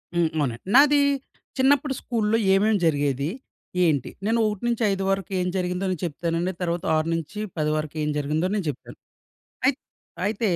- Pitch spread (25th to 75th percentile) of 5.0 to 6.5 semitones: Yes, wide, 5.5 semitones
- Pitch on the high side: No, medium, 180 Hz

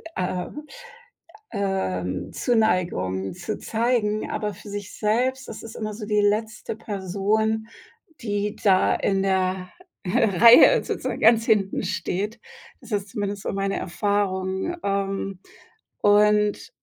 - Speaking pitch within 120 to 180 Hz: No, high, 205 Hz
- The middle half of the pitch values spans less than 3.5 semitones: Yes, narrow, 2.4 semitones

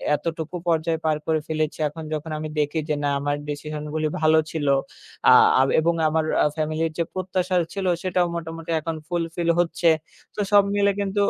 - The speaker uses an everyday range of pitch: No, narrow, 2.1 semitones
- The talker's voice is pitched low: No, medium, 160 Hz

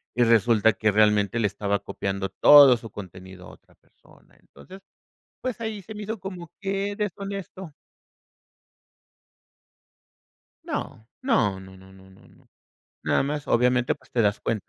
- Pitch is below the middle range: Yes, low, 115 Hz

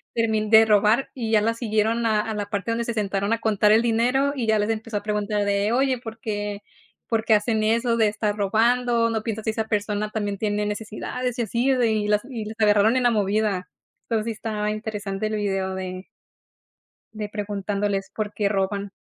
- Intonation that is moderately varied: No, narrow, 1.7 semitones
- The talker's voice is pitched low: No, high, 215 Hz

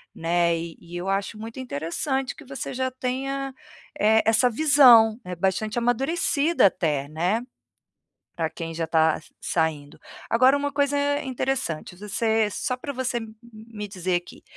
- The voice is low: No, high, 220 Hz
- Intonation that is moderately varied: No, wide, 7.0 semitones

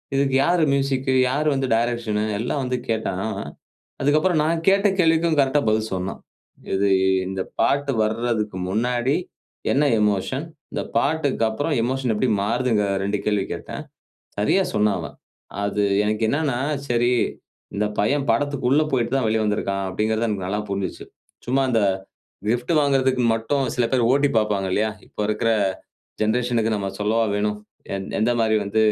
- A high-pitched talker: No, low, 115 Hz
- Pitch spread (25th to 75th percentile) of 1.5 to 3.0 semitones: No, average, 4.3 semitones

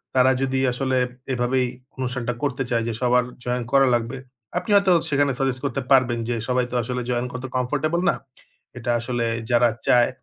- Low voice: Yes, low, 125 Hz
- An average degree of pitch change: No, narrow, 1.6 semitones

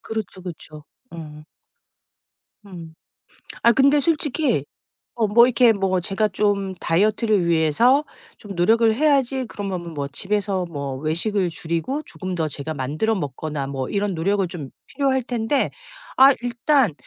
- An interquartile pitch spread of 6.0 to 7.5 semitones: Yes, wide, 6.4 semitones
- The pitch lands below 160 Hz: No, high, 195 Hz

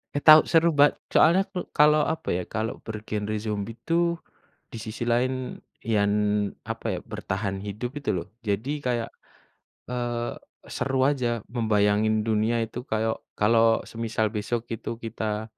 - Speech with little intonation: No, average, 3.1 semitones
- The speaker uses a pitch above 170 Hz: No, low, 115 Hz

